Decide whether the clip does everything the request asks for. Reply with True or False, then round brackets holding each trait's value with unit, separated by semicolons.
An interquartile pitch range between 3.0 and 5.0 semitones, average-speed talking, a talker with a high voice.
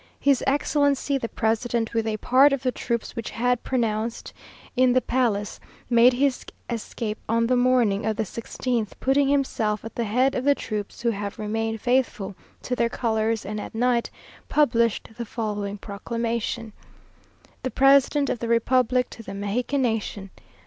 False (2.6 semitones; 165 wpm; 235 Hz)